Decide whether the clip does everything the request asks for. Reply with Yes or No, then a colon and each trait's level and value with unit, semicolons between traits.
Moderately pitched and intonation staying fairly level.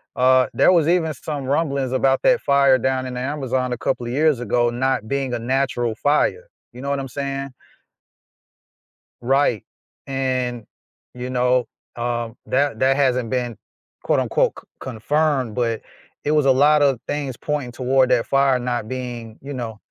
No: low, 130 Hz; narrow, 2.3 semitones